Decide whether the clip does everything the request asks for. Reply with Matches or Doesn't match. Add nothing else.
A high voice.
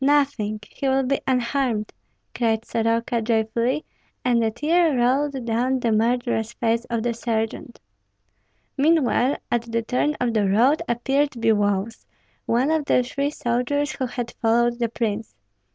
Matches